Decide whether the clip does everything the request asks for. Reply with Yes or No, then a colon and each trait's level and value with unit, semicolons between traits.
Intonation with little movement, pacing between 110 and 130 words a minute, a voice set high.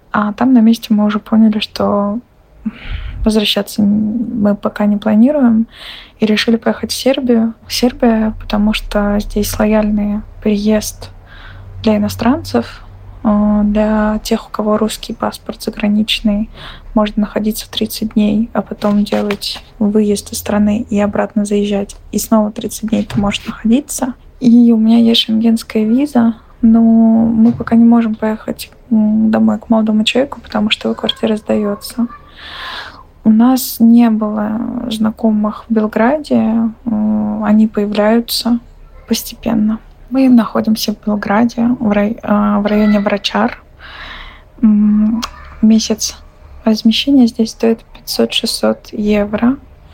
Yes: narrow, 1.6 semitones; average, 120 wpm; high, 220 Hz